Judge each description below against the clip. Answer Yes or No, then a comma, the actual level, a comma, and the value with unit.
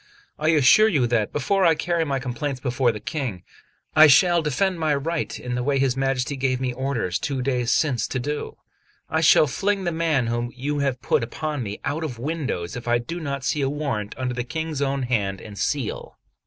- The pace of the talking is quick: Yes, fast, 210 wpm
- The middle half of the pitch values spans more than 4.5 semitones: No, average, 3.9 semitones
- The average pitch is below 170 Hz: Yes, low, 135 Hz